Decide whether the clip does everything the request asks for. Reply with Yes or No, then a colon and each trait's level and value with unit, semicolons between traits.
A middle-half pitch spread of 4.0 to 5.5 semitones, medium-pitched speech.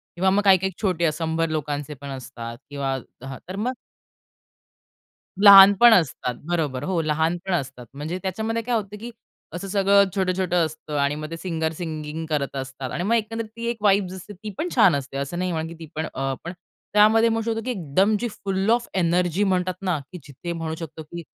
Yes: average, 4.7 semitones; medium, 175 Hz